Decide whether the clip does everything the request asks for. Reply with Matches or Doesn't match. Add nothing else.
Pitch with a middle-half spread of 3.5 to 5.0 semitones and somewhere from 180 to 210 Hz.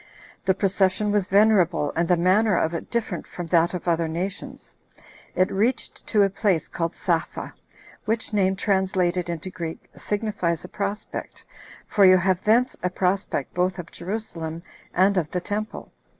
Doesn't match